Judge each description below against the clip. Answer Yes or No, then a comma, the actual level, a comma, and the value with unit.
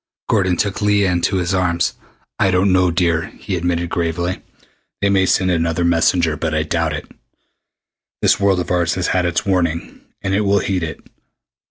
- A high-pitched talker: No, very low, 90 Hz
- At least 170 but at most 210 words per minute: Yes, average, 180 wpm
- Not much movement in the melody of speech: Yes, narrow, 2.1 semitones